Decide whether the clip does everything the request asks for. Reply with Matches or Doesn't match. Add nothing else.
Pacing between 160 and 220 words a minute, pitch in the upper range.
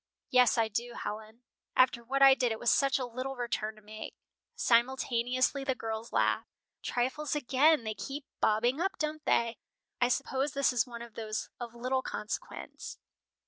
Matches